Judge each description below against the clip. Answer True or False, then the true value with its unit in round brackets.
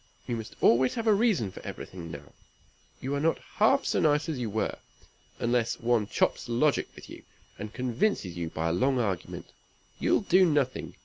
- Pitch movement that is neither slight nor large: False (6.5 semitones)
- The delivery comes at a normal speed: True (185 wpm)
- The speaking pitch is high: False (125 Hz)